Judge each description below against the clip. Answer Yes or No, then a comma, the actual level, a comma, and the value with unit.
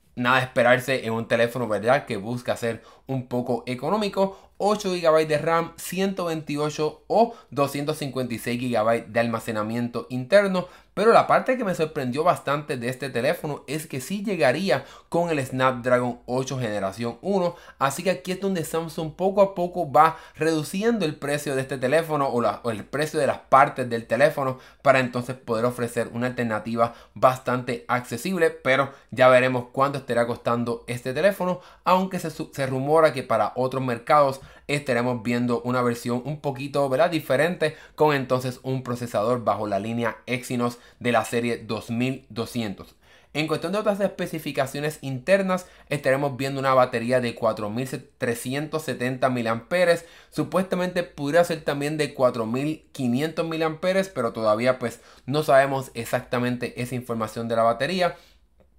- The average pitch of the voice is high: No, low, 135 Hz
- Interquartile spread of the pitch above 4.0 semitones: Yes, average, 4.9 semitones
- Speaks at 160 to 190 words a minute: No, average, 150 wpm